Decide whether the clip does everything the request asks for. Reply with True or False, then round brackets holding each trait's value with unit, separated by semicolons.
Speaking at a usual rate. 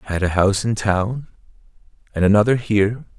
True (170 wpm)